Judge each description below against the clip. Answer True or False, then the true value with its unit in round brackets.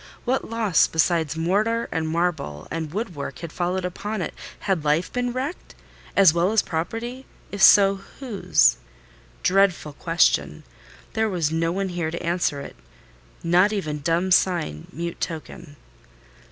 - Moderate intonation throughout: True (4.2 semitones)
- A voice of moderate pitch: True (175 Hz)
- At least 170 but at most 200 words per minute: False (140 wpm)